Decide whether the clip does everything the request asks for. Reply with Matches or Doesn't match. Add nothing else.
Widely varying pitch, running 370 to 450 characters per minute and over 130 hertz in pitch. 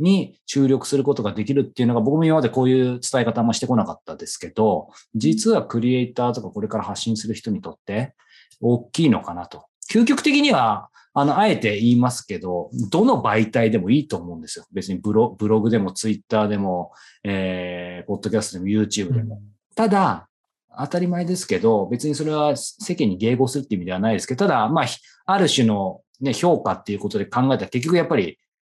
Doesn't match